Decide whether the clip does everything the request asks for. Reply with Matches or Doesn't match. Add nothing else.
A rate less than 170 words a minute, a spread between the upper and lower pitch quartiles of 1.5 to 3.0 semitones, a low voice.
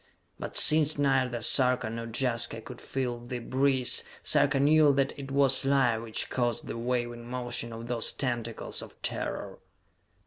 Matches